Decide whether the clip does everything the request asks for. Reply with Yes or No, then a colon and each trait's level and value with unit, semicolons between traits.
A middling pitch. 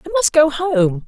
No: very high, 295 Hz